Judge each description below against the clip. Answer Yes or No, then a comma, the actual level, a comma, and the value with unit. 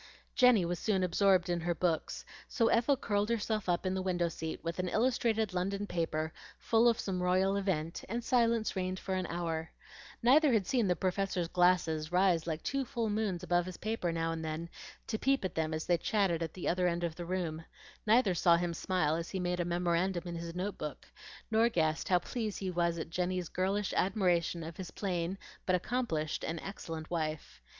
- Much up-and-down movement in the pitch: No, average, 3.2 semitones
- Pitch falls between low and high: Yes, medium, 180 Hz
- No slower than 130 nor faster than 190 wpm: No, fast, 205 wpm